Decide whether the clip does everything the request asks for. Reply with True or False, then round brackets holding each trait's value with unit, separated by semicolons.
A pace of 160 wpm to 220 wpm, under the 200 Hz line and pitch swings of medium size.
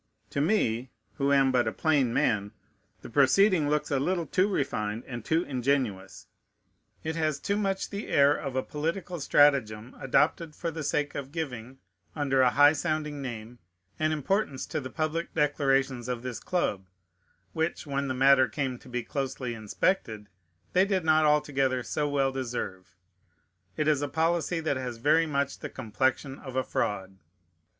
True (165 wpm; 140 Hz; 3.8 semitones)